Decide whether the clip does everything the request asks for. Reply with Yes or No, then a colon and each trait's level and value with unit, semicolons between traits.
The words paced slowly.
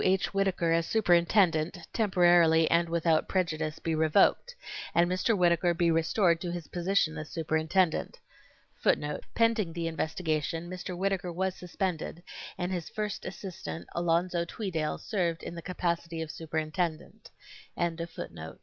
Yes: slow, 125 wpm